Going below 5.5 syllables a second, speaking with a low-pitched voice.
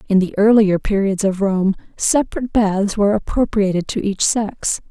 No: 5.0 syllables/s; high, 205 Hz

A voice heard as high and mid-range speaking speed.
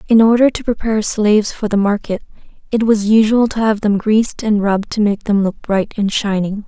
No: high, 210 Hz; fast, 215 wpm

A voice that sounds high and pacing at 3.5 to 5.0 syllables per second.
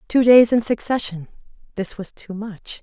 Yes: high, 215 Hz; 4.6 syllables/s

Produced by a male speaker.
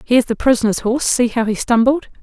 No: female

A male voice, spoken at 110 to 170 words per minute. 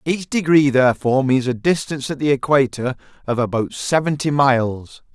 Yes: male; average, 150 wpm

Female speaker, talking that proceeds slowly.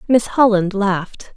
Yes: female; slow, 130 wpm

